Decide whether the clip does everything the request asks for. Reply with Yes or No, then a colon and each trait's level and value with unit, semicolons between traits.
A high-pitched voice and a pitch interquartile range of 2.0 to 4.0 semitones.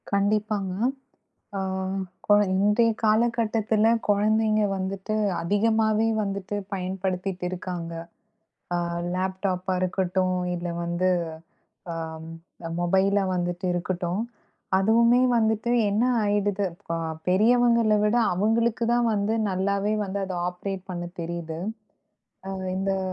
Yes: high, 195 Hz; average, 2.7 semitones